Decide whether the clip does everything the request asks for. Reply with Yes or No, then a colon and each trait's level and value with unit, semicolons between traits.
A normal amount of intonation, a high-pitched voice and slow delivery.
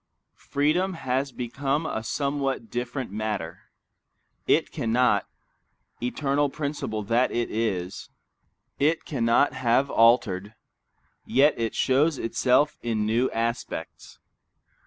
No: average, 3.8 semitones; low, 125 Hz; slow, 100 wpm